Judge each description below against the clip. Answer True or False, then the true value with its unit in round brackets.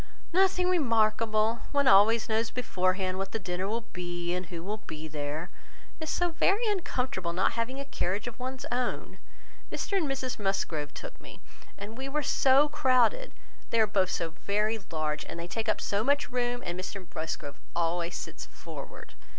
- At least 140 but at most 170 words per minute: False (180 wpm)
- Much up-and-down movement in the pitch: True (6.4 semitones)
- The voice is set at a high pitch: True (215 Hz)